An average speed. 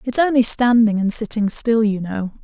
Yes: average, 195 wpm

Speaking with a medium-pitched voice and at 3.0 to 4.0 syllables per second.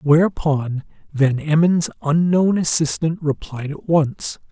Yes: medium, 155 Hz; 3.8 syllables/s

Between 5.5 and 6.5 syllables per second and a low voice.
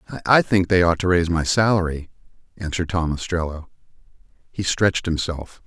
Yes: 6.0 syllables/s; very low, 85 Hz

